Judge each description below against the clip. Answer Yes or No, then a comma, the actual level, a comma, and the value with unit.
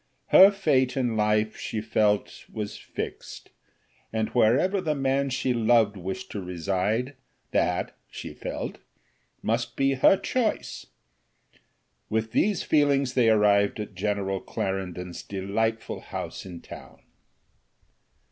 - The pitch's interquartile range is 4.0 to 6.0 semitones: Yes, average, 4.6 semitones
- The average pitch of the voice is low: Yes, low, 110 Hz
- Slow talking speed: Yes, slow, 120 wpm